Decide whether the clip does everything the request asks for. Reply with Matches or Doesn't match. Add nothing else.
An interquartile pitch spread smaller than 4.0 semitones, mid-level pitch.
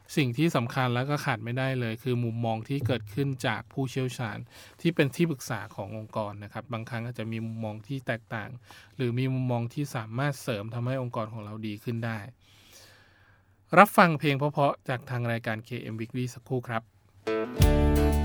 Doesn't match